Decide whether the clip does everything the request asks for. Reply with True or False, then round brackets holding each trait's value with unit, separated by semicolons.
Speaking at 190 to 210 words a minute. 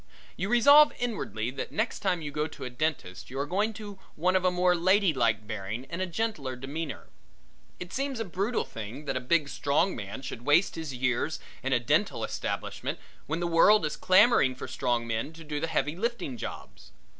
True (200 wpm)